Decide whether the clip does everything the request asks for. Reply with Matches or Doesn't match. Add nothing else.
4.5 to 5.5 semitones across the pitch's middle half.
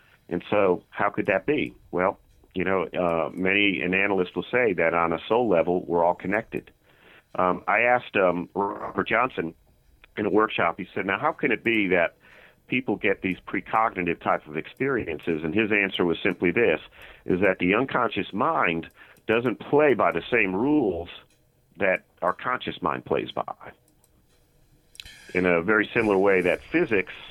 Doesn't match